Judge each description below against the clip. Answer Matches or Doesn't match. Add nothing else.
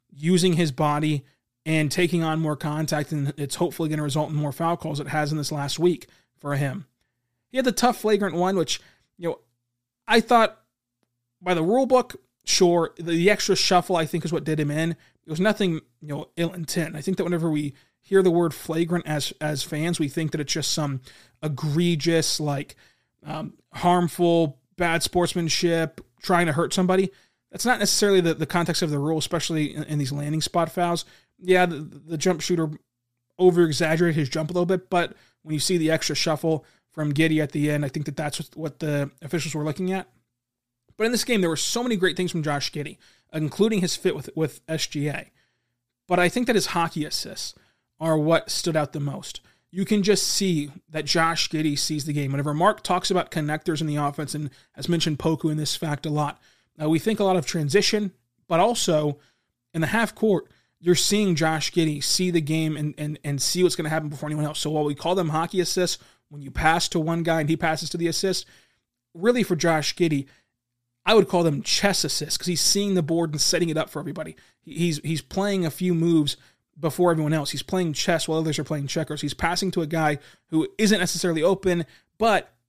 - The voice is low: Doesn't match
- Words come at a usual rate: Doesn't match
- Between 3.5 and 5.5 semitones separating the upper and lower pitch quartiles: Doesn't match